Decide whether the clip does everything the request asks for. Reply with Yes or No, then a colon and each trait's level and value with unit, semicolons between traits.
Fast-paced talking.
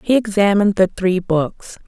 No: average, 160 wpm